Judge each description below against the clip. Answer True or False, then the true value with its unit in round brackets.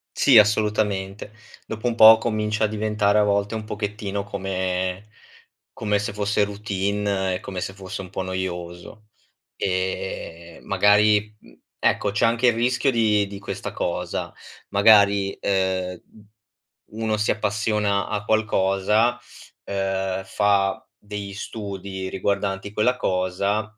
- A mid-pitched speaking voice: False (100 Hz)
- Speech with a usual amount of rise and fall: False (1.8 semitones)